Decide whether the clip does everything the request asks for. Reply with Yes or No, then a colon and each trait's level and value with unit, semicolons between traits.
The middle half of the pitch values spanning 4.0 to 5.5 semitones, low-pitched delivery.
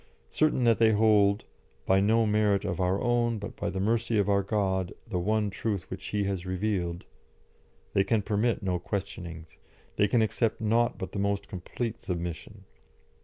No: average, 2.7 semitones; low, 100 Hz